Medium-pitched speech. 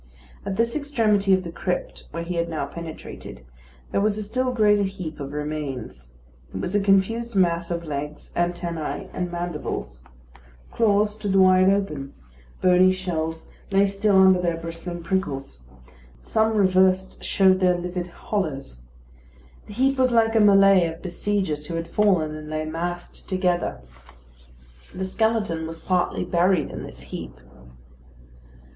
Yes: medium, 180 Hz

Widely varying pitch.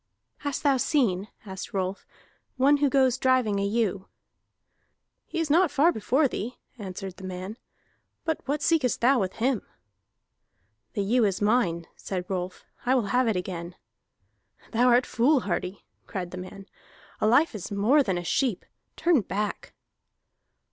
Yes: wide, 5.7 semitones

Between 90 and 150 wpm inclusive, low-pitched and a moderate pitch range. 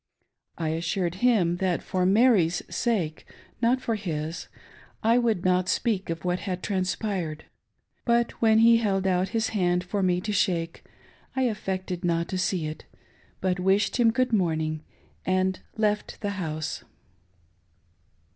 No: average, 145 wpm; medium, 185 Hz; average, 3.9 semitones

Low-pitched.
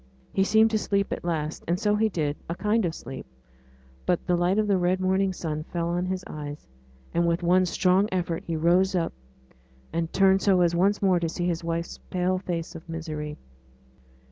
No: medium, 175 Hz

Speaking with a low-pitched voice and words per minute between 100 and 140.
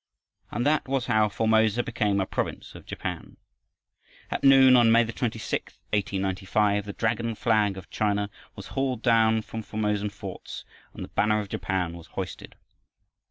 No: low, 110 Hz; average, 155 wpm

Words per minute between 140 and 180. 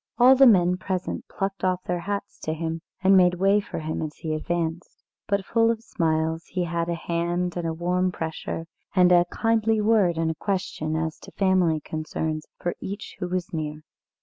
No: average, 195 wpm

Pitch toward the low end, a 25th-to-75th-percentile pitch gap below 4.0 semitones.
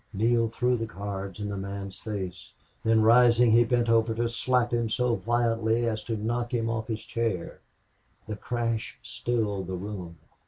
Yes: low, 115 Hz; narrow, 2.5 semitones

